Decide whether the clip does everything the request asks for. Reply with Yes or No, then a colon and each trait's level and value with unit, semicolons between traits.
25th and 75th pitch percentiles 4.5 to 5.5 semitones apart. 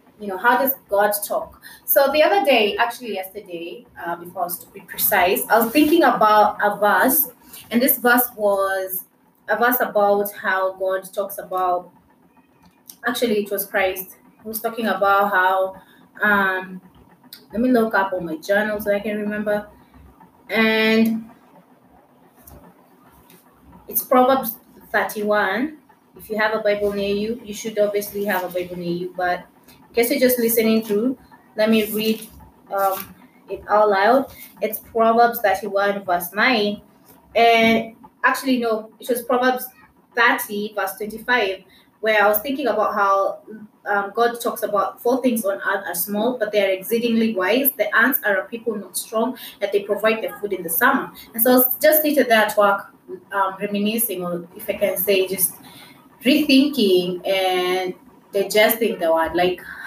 No: average, 3.2 semitones